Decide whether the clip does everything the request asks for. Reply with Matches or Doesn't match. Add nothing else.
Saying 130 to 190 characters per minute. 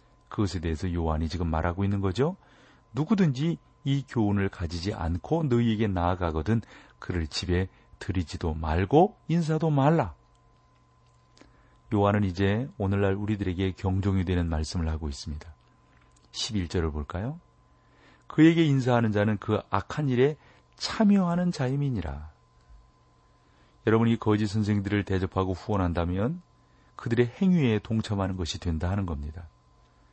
Doesn't match